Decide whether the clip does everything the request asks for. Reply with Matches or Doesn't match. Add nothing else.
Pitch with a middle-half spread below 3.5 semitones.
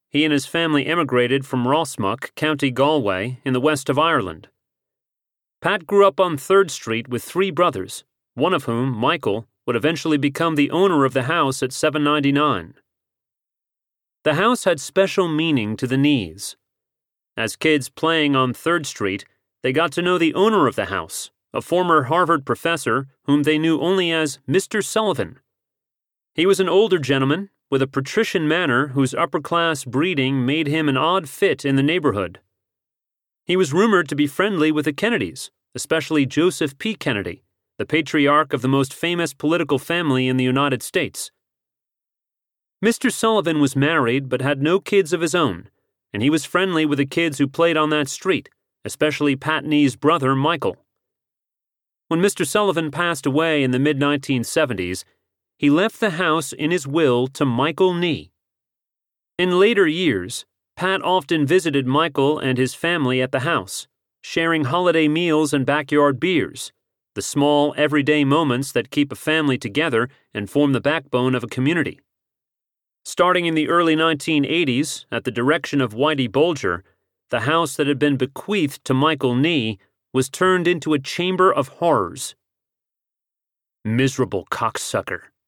Doesn't match